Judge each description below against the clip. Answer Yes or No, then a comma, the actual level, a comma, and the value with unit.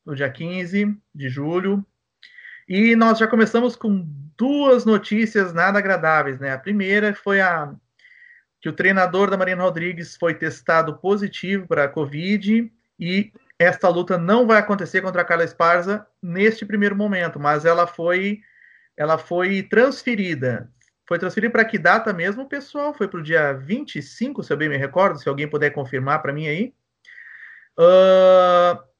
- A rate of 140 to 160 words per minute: Yes, average, 155 wpm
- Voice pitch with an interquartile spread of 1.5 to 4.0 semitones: No, average, 4.7 semitones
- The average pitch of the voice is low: No, high, 190 Hz